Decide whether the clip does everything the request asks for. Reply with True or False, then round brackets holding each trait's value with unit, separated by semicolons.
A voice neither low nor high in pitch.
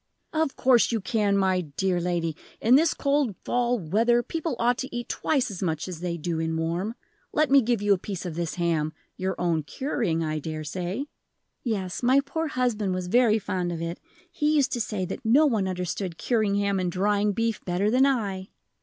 False (200 Hz)